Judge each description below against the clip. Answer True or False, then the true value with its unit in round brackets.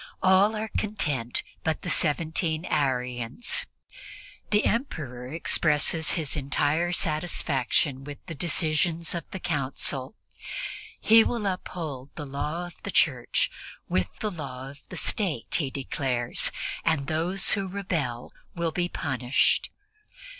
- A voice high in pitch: False (155 Hz)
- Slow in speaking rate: True (125 wpm)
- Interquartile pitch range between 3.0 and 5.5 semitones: True (4.7 semitones)